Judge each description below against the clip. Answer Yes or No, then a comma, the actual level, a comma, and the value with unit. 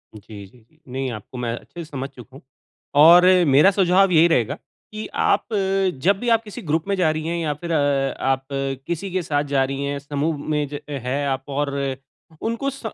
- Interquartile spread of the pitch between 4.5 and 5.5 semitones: Yes, average, 4.8 semitones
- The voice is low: No, medium, 150 Hz